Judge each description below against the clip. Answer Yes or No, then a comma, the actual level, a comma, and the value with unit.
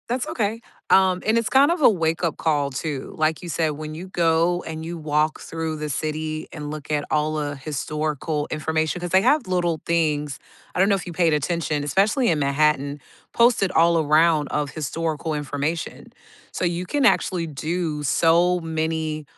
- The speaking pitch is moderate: Yes, medium, 160 Hz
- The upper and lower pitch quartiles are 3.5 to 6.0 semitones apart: No, average, 2.7 semitones